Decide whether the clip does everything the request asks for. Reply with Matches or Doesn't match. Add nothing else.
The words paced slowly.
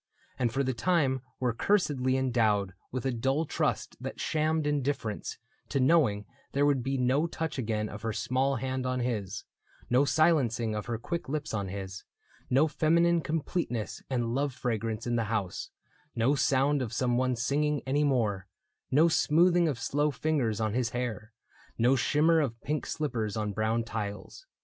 Doesn't match